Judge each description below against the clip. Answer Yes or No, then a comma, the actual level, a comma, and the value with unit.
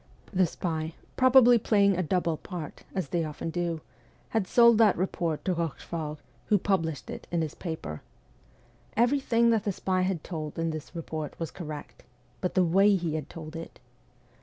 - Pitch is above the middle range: No, medium, 175 Hz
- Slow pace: No, average, 170 wpm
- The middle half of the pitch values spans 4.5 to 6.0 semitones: No, average, 3.7 semitones